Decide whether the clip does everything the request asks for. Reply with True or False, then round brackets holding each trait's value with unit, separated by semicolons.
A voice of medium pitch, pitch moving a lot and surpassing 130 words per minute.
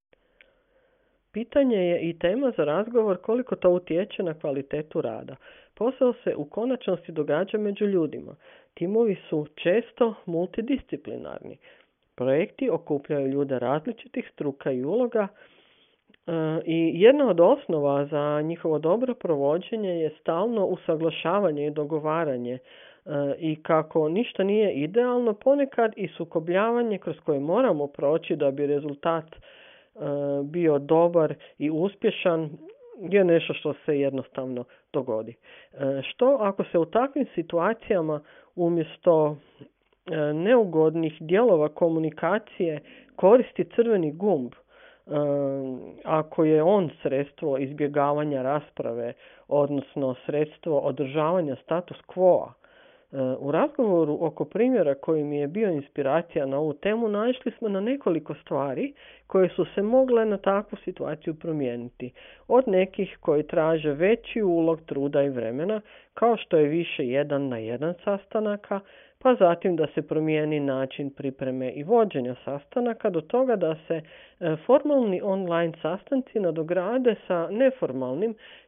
False (165 Hz; 6.5 semitones; 115 wpm)